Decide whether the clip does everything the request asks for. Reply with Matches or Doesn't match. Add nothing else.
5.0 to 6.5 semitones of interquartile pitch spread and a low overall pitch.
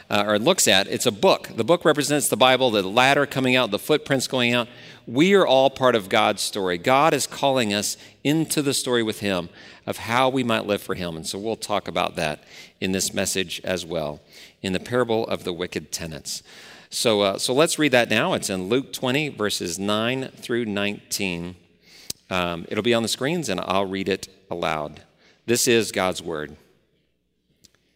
Matches